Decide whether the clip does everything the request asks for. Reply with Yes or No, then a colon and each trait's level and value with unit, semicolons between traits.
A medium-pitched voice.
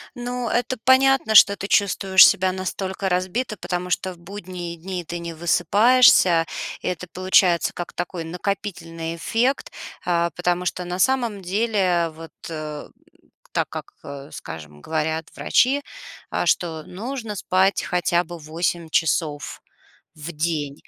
Yes: medium, 180 Hz